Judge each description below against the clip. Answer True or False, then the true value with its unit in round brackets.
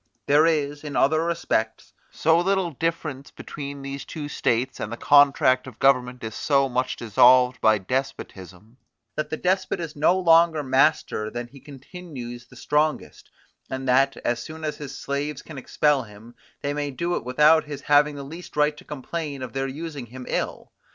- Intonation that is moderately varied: True (3.3 semitones)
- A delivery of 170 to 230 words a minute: True (180 wpm)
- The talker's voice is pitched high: False (140 Hz)